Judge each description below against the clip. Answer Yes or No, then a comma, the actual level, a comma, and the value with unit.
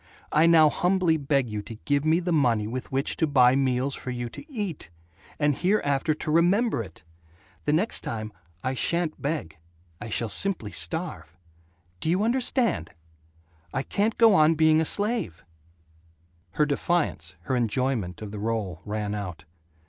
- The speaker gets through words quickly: No, average, 165 wpm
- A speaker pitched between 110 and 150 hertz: Yes, medium, 140 Hz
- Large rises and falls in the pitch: Yes, wide, 7.7 semitones